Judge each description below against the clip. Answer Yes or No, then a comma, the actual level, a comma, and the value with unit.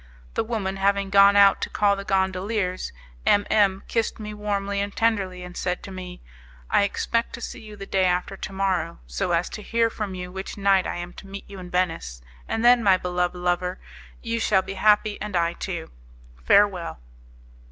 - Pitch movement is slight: Yes, narrow, 2.2 semitones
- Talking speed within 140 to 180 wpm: No, average, 195 wpm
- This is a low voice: No, high, 195 Hz